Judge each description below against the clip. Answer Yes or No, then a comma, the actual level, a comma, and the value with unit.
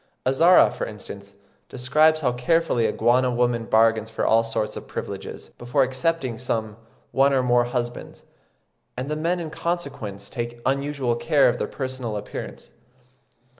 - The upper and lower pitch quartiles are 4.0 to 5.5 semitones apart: No, average, 3.6 semitones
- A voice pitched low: Yes, low, 125 Hz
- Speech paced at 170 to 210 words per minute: No, average, 150 wpm